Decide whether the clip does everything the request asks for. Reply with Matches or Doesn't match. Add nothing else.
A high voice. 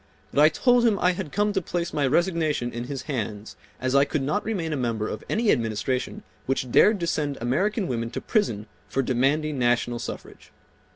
Doesn't match